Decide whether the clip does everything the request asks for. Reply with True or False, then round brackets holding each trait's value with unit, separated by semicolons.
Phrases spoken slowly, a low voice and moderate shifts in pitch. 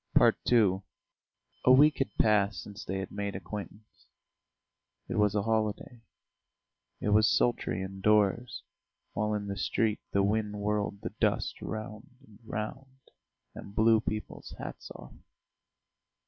False (130 wpm; 105 Hz; 1.6 semitones)